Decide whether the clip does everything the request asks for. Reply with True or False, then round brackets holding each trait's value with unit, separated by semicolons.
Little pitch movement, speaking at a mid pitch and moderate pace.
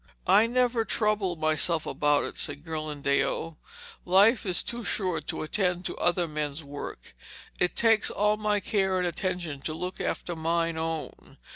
False (4.7 semitones; 175 Hz; 155 wpm)